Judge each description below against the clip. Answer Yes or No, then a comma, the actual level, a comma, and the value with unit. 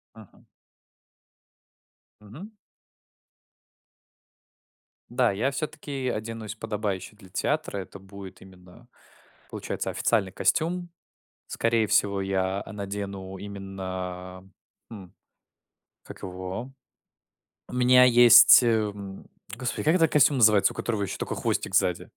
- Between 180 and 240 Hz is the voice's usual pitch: No, low, 105 Hz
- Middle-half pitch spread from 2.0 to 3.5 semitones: No, average, 4.0 semitones